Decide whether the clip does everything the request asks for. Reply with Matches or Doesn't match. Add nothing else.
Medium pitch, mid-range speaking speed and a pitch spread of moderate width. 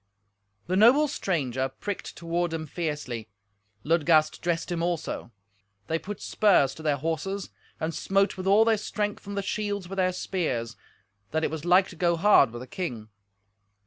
Matches